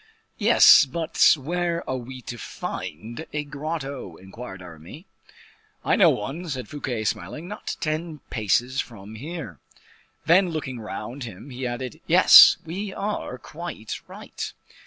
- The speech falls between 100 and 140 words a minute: Yes, slow, 135 wpm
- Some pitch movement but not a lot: No, wide, 6.2 semitones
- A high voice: No, low, 130 Hz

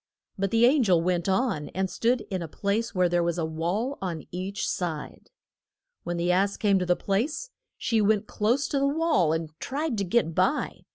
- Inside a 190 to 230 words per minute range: Yes, fast, 205 wpm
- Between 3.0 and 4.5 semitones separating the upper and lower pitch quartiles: No, average, 5.3 semitones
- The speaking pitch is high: Yes, high, 195 Hz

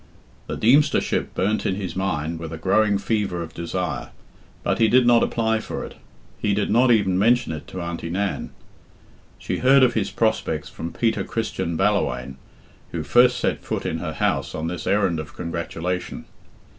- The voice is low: Yes, very low, 95 Hz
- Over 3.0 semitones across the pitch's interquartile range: Yes, average, 5.1 semitones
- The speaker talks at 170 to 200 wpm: Yes, average, 180 wpm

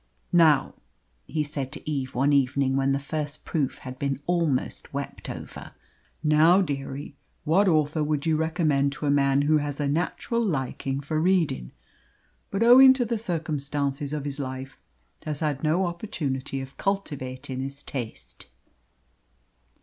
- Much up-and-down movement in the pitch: No, average, 2.9 semitones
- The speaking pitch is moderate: Yes, medium, 145 Hz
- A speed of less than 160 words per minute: Yes, average, 150 wpm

